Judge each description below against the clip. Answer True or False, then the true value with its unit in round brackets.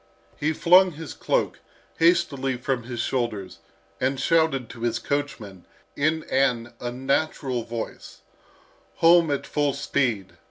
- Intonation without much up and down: False (4.7 semitones)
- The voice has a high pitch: False (135 Hz)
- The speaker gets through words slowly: True (120 wpm)